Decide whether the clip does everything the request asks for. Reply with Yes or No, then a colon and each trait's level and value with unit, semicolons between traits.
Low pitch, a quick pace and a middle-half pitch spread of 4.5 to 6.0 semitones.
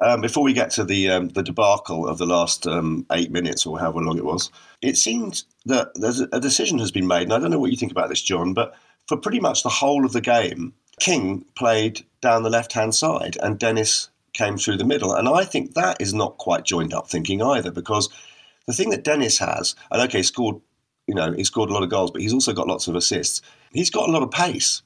Yes: low, 105 Hz; fast, 250 wpm; average, 4.8 semitones